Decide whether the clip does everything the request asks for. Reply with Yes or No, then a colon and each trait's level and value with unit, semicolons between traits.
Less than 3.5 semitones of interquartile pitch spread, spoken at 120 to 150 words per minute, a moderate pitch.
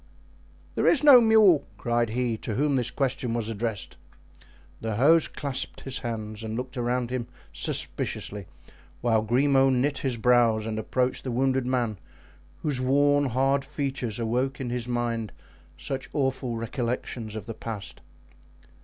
No: average, 2.8 semitones; average, 145 wpm; low, 125 Hz